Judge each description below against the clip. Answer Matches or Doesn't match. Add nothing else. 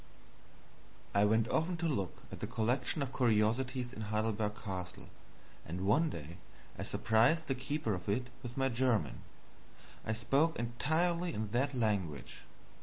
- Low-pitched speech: Matches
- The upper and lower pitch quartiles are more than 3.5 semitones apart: Matches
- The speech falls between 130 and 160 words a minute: Matches